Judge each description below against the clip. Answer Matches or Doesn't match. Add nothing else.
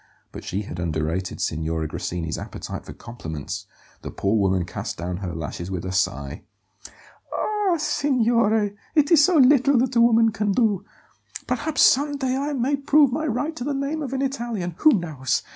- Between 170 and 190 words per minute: Matches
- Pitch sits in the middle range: Doesn't match